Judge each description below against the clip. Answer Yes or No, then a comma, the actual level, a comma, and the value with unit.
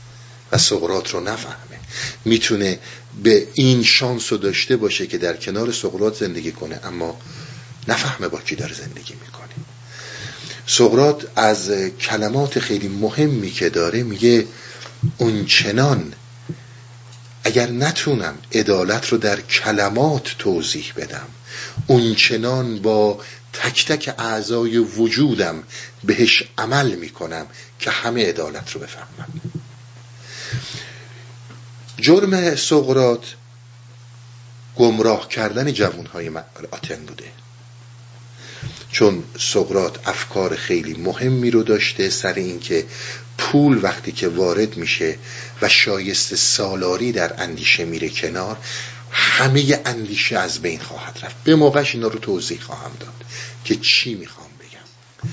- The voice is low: Yes, low, 120 Hz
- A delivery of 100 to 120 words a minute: Yes, average, 110 wpm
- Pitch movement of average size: No, narrow, 2.2 semitones